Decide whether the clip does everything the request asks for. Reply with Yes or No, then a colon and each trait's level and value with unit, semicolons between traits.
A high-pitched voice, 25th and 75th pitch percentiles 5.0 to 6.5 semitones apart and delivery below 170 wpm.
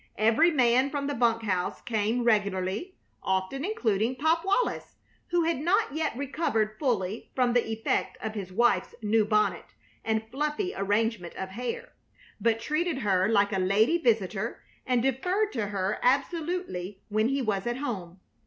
Yes: high, 230 Hz; wide, 5.5 semitones; average, 155 wpm